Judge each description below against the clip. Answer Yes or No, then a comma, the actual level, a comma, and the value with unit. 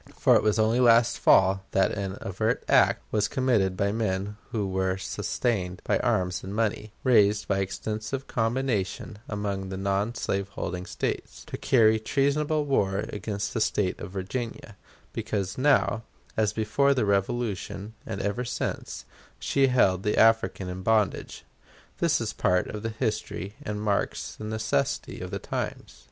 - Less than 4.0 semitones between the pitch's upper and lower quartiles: Yes, average, 2.8 semitones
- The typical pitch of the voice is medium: No, low, 105 Hz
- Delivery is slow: No, average, 155 wpm